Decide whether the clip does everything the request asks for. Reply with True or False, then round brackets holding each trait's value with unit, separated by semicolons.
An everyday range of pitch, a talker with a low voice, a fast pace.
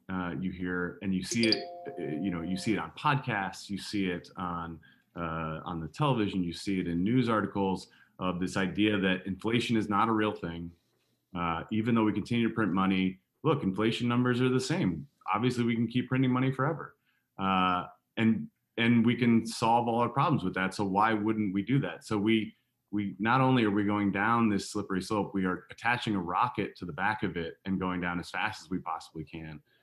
True (4.0 semitones; 100 Hz; 215 wpm)